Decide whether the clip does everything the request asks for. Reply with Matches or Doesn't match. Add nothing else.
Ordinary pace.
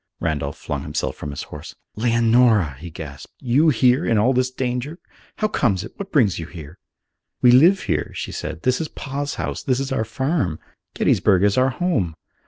Matches